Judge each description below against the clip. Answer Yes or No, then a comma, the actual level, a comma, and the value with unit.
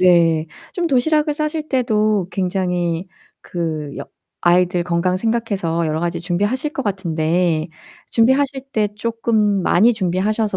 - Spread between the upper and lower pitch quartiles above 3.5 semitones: Yes, average, 5.1 semitones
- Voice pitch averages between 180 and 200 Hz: Yes, high, 190 Hz